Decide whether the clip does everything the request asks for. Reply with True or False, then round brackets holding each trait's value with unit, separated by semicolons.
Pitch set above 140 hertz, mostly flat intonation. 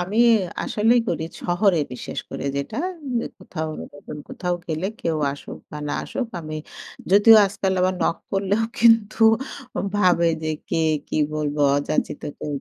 False (185 Hz; 4.7 semitones)